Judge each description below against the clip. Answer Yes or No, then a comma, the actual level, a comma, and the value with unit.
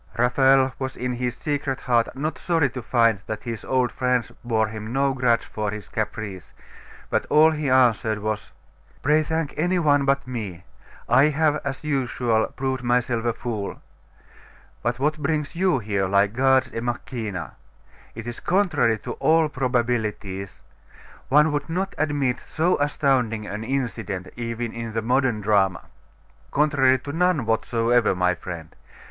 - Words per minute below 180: Yes, average, 155 wpm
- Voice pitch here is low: Yes, low, 125 Hz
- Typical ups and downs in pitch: Yes, average, 4.3 semitones